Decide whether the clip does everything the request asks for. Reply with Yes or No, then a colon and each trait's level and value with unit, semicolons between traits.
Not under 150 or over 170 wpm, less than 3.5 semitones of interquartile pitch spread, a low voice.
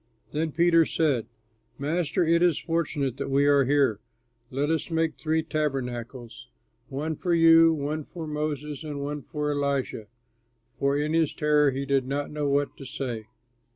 No: average, 160 wpm; narrow, 2.6 semitones; medium, 145 Hz